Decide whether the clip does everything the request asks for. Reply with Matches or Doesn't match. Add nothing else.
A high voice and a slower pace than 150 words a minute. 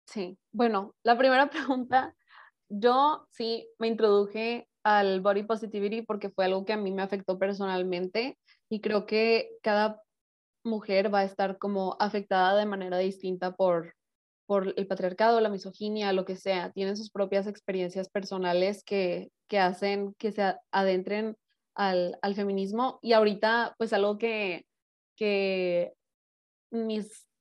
Matches